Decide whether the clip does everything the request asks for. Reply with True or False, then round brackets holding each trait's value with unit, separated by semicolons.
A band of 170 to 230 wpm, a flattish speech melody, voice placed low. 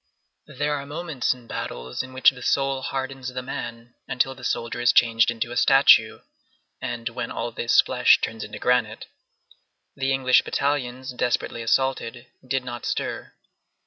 False (155 wpm; 2.2 semitones; 125 Hz)